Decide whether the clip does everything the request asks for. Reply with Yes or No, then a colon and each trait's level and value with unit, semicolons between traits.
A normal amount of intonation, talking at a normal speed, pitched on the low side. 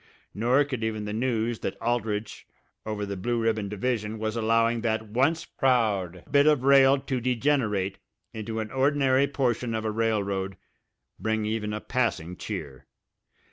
Yes: average, 3.3 semitones; average, 155 wpm; low, 115 Hz